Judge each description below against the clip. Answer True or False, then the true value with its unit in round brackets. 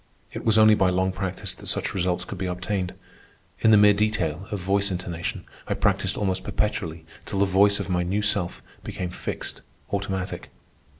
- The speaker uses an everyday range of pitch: False (2.3 semitones)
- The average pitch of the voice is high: False (95 Hz)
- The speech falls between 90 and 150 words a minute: False (180 wpm)